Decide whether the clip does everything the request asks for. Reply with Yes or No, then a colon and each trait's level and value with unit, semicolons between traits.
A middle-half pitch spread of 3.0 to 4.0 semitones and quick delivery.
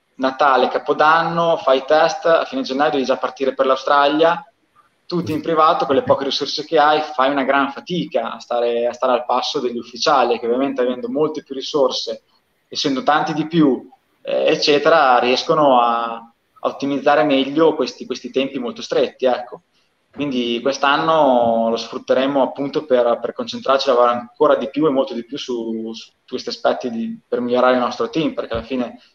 Yes: average, 3.7 semitones; fast, 175 wpm